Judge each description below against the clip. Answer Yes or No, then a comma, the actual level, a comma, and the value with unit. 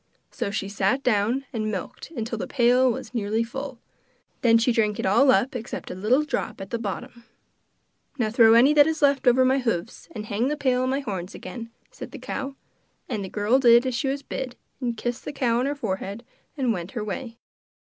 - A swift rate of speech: Yes, fast, 215 wpm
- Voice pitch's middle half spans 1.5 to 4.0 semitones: Yes, average, 3.5 semitones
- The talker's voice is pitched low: No, high, 235 Hz